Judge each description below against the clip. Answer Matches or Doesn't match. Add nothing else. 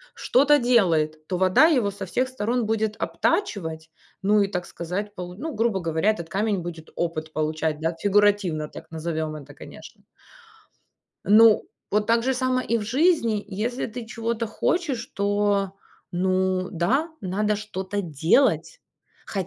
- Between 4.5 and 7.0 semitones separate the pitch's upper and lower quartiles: Matches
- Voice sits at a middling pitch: Doesn't match